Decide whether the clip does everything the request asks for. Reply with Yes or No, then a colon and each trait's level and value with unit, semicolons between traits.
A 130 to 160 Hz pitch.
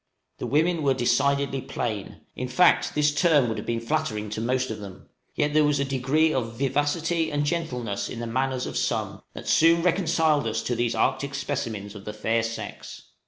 Yes: low, 135 Hz